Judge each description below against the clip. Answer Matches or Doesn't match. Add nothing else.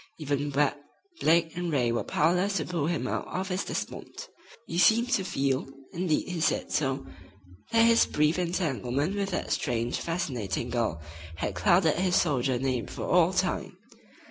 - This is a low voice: Doesn't match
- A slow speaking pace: Doesn't match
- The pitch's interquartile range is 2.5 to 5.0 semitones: Doesn't match